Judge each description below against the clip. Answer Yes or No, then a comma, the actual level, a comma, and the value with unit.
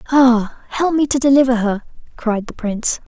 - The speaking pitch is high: Yes, very high, 250 Hz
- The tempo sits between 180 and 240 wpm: No, average, 170 wpm